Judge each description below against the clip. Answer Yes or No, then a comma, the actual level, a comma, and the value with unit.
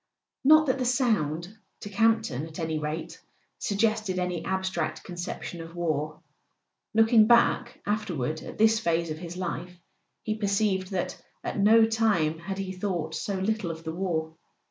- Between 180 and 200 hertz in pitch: Yes, medium, 185 Hz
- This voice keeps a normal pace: Yes, average, 165 wpm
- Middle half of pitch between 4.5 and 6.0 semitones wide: Yes, average, 4.9 semitones